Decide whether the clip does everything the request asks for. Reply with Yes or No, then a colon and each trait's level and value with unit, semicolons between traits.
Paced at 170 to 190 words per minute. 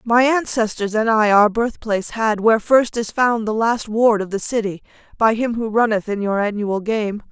No: fast, 205 wpm